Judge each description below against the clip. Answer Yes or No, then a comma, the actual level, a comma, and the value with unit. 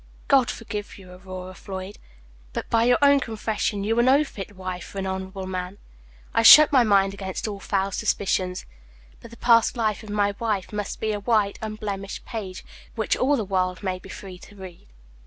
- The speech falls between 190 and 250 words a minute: Yes, average, 195 wpm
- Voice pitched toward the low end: No, high, 205 Hz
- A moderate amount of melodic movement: Yes, average, 3.0 semitones